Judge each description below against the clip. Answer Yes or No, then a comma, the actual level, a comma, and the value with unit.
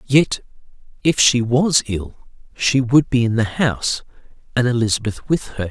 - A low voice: Yes, low, 120 Hz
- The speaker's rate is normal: Yes, average, 160 wpm